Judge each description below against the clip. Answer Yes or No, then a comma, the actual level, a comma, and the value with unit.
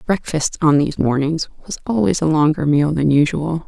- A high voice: No, medium, 155 Hz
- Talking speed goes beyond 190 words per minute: No, average, 180 wpm